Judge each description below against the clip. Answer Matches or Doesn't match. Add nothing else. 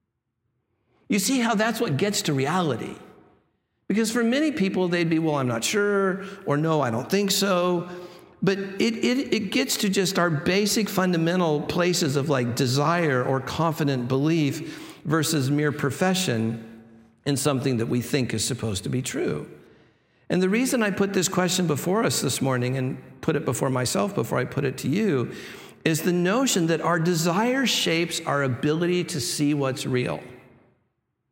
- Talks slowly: Doesn't match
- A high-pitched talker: Doesn't match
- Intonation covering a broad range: Matches